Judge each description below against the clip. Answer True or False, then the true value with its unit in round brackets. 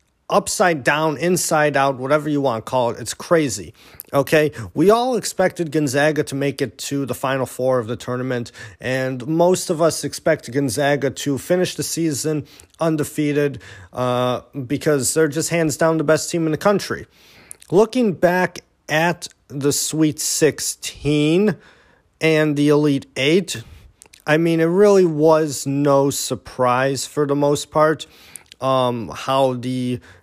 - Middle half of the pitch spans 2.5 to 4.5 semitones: True (3.6 semitones)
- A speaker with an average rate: True (145 wpm)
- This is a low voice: False (145 Hz)